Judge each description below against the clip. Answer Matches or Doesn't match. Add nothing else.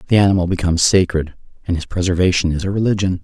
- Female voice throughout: Doesn't match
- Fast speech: Doesn't match